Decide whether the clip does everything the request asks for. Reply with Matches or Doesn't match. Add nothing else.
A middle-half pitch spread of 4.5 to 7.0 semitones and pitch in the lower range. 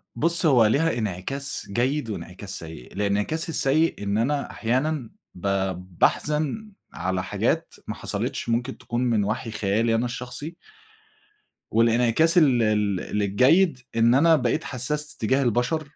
Matches